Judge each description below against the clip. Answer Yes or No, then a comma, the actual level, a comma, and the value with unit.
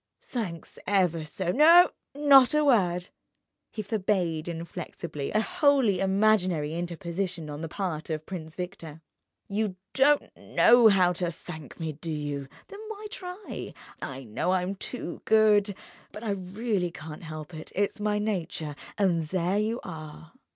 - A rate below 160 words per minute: Yes, average, 140 wpm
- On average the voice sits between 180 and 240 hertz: Yes, medium, 185 Hz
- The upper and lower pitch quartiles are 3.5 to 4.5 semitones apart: No, average, 4.9 semitones